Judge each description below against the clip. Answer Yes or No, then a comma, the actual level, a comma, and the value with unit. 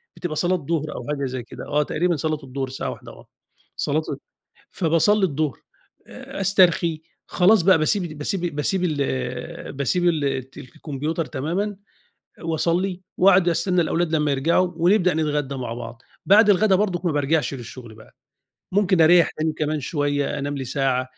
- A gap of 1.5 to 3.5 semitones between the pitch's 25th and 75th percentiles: No, average, 4.1 semitones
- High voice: No, medium, 155 Hz